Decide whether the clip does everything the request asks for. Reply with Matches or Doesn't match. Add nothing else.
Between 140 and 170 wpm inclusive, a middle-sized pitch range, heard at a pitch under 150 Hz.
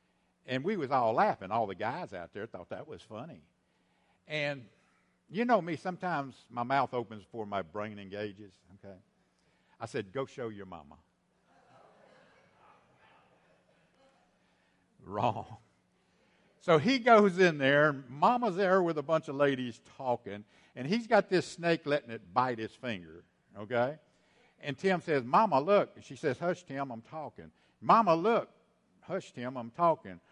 Doesn't match